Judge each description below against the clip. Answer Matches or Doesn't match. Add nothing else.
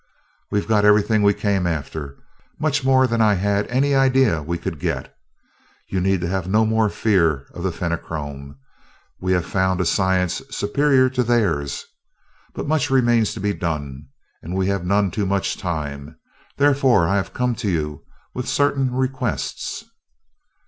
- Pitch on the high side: Doesn't match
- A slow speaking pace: Doesn't match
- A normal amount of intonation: Doesn't match